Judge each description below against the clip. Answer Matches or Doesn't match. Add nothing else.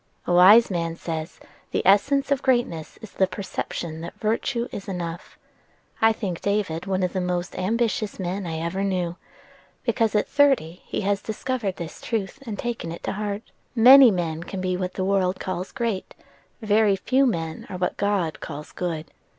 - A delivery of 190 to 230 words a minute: Doesn't match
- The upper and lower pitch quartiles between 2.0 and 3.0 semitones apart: Doesn't match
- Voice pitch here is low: Doesn't match